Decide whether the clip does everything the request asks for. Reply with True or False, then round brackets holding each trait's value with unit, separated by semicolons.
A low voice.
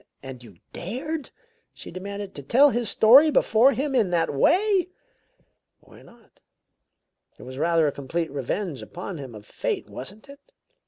False (200 Hz)